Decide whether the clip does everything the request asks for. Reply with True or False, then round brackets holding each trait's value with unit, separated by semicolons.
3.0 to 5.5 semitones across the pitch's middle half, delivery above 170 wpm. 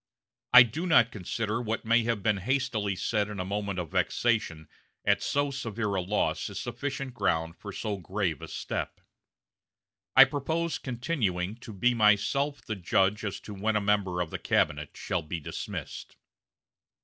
False (4.2 semitones; 165 wpm)